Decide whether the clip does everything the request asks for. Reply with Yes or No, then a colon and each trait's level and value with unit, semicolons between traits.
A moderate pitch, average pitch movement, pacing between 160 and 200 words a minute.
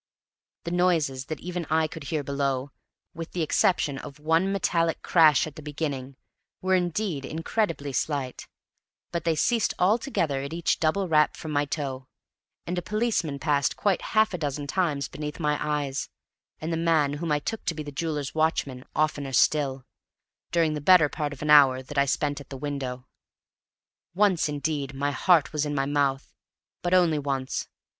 Yes: medium, 150 Hz; average, 3.1 semitones; average, 175 wpm